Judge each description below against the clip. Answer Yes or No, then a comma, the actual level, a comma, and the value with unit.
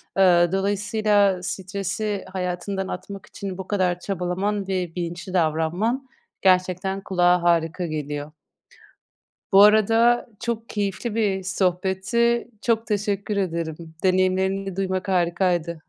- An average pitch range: No, narrow, 2.3 semitones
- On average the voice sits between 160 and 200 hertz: Yes, high, 190 Hz